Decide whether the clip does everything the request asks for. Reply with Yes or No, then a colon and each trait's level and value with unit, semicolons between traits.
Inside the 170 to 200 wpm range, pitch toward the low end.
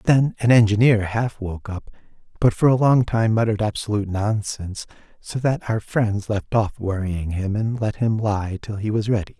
Yes: average, 190 wpm; low, 110 Hz